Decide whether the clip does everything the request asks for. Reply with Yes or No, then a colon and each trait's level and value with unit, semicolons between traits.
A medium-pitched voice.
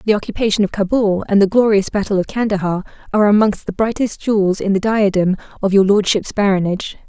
No: high, 200 Hz